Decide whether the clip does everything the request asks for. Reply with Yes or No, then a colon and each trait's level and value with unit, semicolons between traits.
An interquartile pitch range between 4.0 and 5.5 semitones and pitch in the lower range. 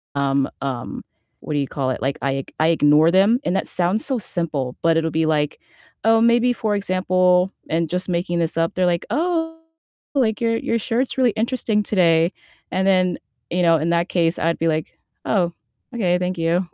No: average, 4.5 semitones; medium, 175 Hz